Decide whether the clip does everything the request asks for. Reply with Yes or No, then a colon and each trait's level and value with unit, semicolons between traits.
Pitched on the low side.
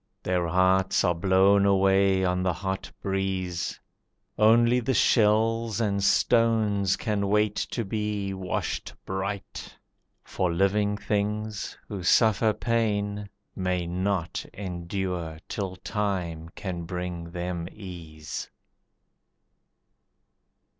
Yes: very low, 95 Hz